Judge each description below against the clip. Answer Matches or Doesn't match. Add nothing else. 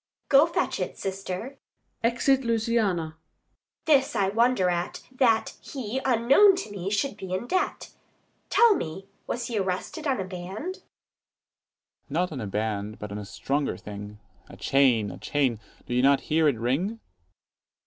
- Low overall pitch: Doesn't match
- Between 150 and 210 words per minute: Matches